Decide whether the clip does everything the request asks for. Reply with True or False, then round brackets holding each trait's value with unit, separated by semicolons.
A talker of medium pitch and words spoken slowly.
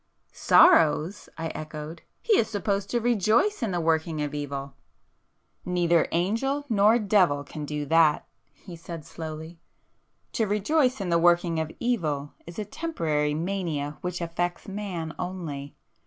True (170 Hz; 130 wpm)